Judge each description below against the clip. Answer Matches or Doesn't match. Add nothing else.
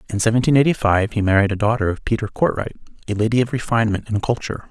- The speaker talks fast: Matches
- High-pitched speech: Doesn't match